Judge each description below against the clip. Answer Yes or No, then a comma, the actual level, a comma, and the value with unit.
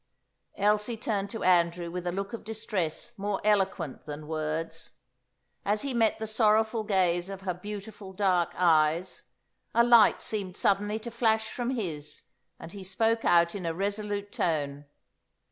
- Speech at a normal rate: Yes, average, 155 wpm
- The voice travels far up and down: No, average, 4.0 semitones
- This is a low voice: No, high, 195 Hz